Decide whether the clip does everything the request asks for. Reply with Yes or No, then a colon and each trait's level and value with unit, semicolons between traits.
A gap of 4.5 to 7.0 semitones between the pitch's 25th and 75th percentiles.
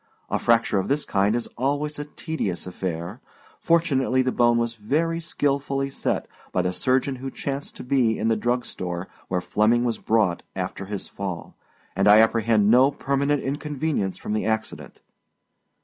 Yes: average, 5.1 semitones